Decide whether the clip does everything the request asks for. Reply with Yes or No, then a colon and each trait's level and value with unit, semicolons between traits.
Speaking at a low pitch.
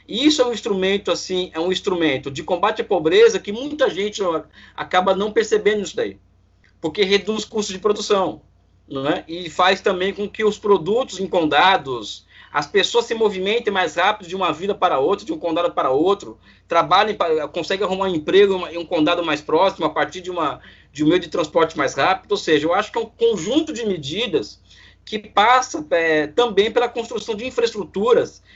No: high, 195 Hz